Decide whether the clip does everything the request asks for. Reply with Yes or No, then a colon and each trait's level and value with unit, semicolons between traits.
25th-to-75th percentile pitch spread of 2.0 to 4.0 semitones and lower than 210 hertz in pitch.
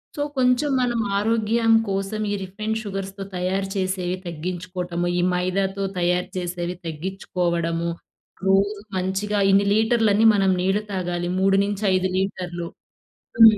Yes: narrow, 2.5 semitones; high, 190 Hz